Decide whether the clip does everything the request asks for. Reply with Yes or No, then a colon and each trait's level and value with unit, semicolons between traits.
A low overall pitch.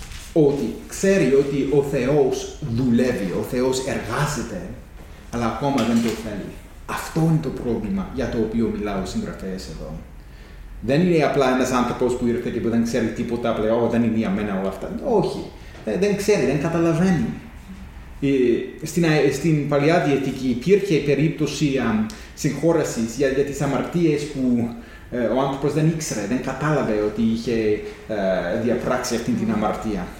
Yes: low, 125 Hz